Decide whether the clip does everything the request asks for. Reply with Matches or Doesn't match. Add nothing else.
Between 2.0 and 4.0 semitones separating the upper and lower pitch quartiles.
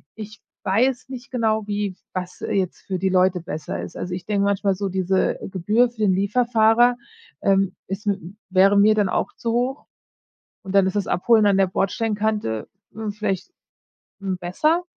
Matches